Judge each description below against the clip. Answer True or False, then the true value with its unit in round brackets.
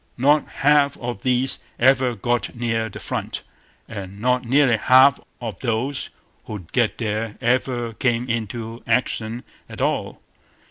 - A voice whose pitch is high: False (120 Hz)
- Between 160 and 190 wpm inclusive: False (140 wpm)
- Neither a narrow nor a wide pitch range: False (2.3 semitones)